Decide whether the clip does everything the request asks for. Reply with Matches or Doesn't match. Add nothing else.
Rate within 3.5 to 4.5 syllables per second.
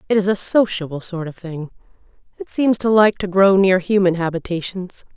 Doesn't match